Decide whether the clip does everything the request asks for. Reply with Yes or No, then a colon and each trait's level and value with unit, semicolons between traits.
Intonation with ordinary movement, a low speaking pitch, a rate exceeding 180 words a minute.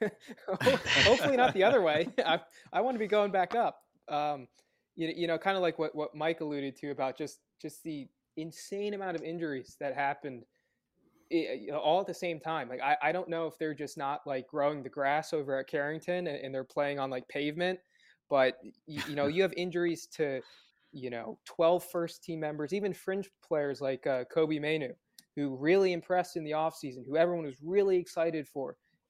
No: average, 3.7 semitones; medium, 160 Hz; average, 200 wpm